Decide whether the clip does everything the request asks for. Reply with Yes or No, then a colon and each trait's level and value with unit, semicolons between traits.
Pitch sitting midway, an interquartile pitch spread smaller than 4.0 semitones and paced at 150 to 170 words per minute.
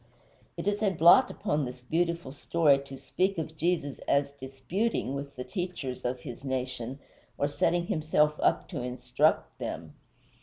No: medium, 145 Hz; average, 4.8 semitones; average, 155 wpm